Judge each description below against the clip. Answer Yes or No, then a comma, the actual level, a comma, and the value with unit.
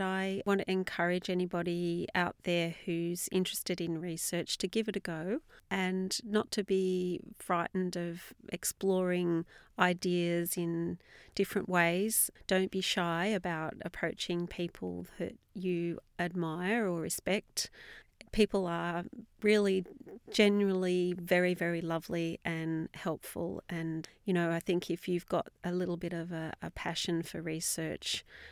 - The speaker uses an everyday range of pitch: No, narrow, 1.9 semitones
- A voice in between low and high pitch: Yes, medium, 175 Hz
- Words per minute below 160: Yes, slow, 135 wpm